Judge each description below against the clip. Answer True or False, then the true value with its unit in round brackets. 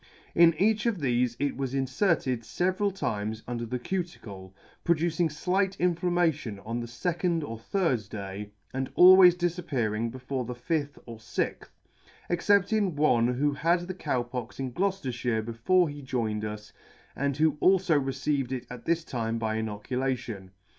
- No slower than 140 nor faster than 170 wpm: True (155 wpm)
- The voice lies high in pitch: False (135 Hz)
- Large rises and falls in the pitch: True (6.9 semitones)